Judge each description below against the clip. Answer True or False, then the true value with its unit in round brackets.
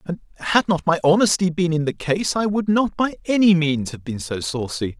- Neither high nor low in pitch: True (170 Hz)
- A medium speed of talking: False (230 wpm)